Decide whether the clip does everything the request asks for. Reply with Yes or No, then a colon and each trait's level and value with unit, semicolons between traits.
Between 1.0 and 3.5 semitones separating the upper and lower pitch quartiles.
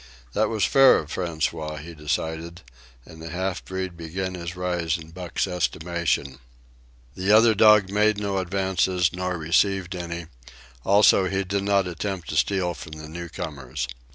Yes: average, 2.9 semitones